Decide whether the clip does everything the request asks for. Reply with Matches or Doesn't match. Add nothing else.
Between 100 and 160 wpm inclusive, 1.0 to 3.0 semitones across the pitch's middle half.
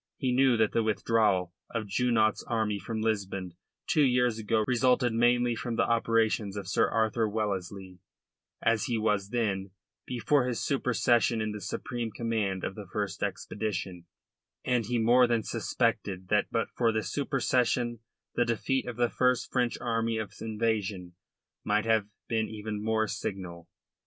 Matches